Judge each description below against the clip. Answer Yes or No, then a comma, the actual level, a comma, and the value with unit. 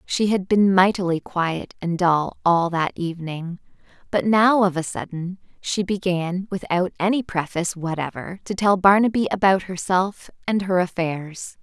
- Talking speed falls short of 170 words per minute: Yes, average, 150 wpm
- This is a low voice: No, medium, 185 Hz